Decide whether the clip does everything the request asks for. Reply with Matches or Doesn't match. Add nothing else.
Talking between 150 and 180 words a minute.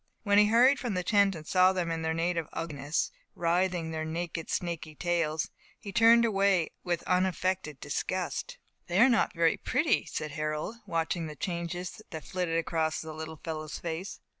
Matches